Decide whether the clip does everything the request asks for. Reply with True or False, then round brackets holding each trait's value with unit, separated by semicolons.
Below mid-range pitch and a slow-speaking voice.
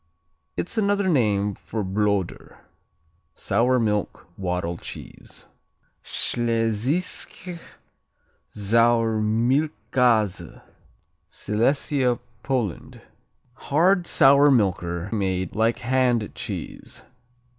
True (115 Hz; 70 wpm)